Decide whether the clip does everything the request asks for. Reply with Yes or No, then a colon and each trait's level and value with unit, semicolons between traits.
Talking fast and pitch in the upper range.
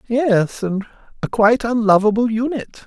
No: slow, 125 wpm; high, 225 Hz